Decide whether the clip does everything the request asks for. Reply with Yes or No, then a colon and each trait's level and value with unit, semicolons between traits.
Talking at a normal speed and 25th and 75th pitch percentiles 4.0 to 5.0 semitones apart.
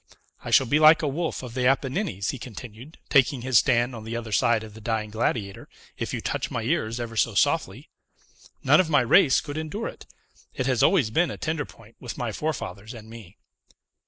No: fast, 210 wpm; average, 4.7 semitones